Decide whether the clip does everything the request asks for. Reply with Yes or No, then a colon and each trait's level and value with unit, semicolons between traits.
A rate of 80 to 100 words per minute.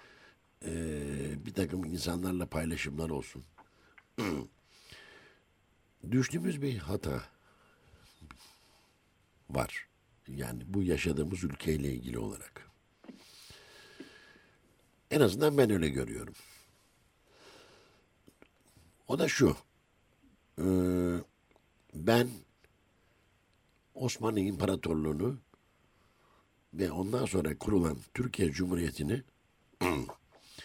No: slow, 65 wpm